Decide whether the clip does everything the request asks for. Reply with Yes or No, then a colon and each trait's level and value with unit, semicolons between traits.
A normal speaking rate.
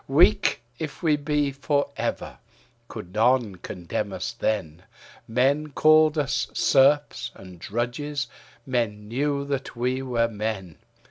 No: slow, 125 wpm